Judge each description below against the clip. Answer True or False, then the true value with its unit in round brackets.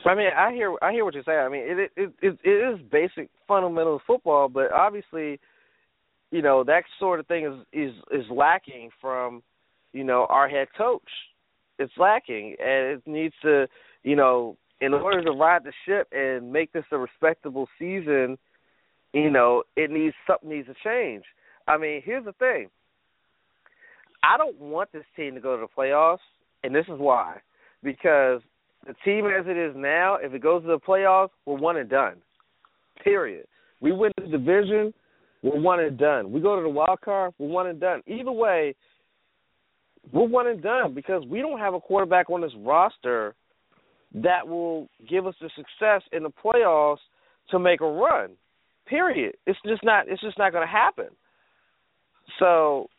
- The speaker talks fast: False (180 wpm)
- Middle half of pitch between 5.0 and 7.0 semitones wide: True (5.6 semitones)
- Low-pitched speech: False (165 Hz)